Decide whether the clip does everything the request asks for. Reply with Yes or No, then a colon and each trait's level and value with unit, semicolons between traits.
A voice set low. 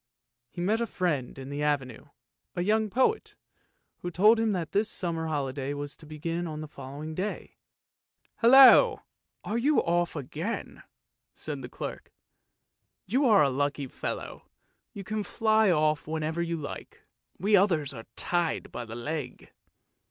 No: medium, 165 Hz